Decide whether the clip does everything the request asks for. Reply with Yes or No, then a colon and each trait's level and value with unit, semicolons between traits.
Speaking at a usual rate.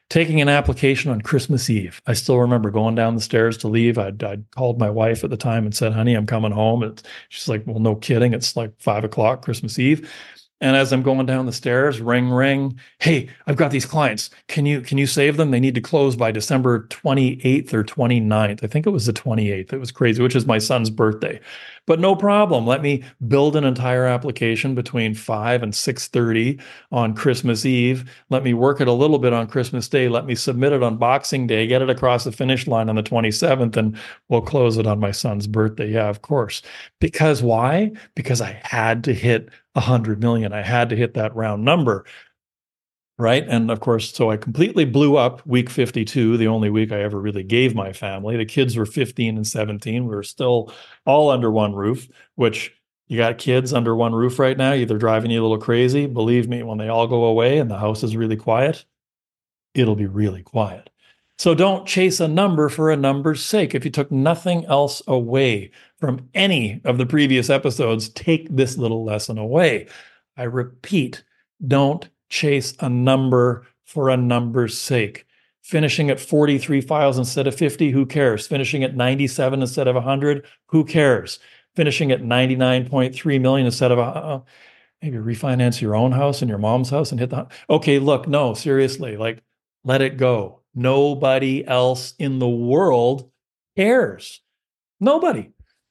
Yes: average, 195 wpm